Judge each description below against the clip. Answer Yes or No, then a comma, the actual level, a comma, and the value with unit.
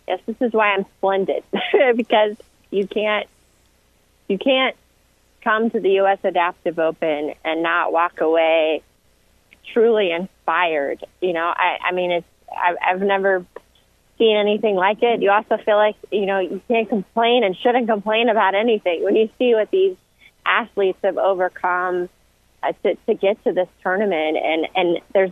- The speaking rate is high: No, average, 160 wpm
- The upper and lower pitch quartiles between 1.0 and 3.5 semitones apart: No, average, 4.0 semitones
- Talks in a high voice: Yes, high, 195 Hz